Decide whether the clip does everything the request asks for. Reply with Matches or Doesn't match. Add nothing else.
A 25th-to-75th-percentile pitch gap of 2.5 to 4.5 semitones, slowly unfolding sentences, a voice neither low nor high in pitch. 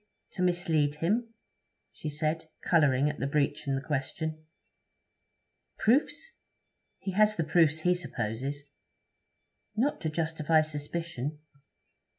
Matches